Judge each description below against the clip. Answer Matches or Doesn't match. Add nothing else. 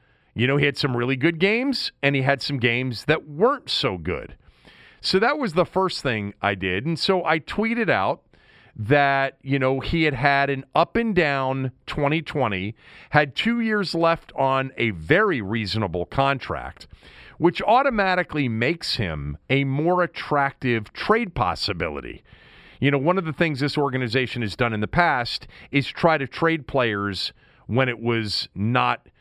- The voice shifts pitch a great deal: Matches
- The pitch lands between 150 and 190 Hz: Doesn't match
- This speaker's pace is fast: Doesn't match